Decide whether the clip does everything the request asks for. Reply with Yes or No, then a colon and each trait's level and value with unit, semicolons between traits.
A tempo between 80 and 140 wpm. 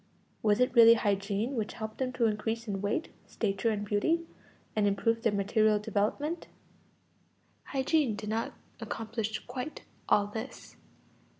Yes: slow, 135 wpm